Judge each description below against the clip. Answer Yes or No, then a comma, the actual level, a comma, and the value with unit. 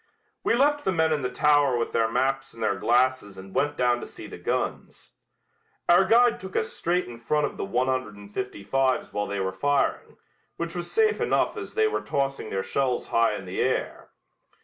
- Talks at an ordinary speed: No, fast, 215 wpm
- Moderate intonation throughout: No, wide, 6.3 semitones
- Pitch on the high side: No, low, 130 Hz